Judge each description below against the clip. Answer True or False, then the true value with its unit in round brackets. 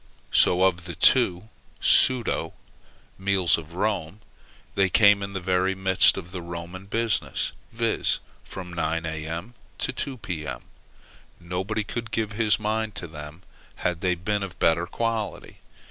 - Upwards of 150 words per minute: False (145 wpm)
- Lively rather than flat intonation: False (3.9 semitones)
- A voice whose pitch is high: False (95 Hz)